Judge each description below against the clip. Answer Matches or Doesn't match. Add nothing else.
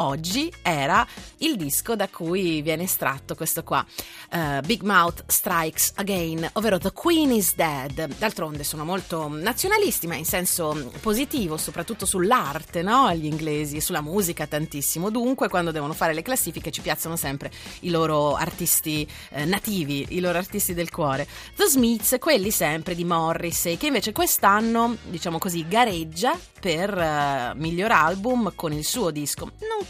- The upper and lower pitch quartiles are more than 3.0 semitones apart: Matches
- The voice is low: Doesn't match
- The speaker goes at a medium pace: Matches